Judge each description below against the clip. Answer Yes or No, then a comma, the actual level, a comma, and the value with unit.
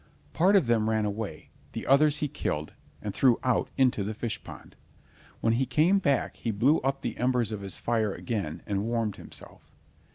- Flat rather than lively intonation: No, average, 4.3 semitones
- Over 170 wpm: Yes, average, 190 wpm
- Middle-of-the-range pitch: No, low, 115 Hz